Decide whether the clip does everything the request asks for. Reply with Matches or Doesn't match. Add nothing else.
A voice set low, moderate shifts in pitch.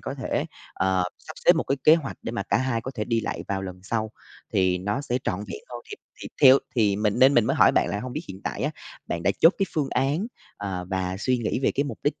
Doesn't match